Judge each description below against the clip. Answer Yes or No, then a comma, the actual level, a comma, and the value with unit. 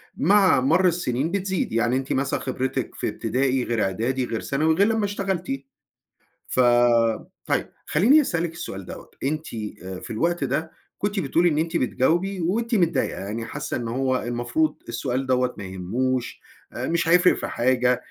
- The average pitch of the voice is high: No, medium, 140 Hz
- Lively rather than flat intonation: Yes, wide, 5.9 semitones